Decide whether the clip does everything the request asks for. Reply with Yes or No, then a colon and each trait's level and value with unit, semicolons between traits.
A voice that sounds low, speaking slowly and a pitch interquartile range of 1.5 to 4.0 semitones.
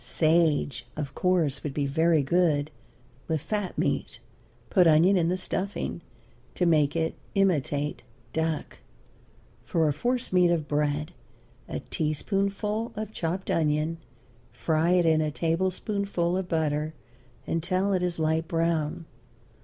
No: medium, 165 Hz; slow, 130 wpm; average, 3.2 semitones